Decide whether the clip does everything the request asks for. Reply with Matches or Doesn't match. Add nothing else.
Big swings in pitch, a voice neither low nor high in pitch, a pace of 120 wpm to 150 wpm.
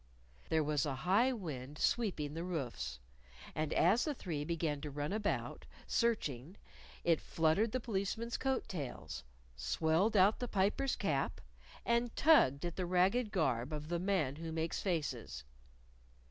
Matches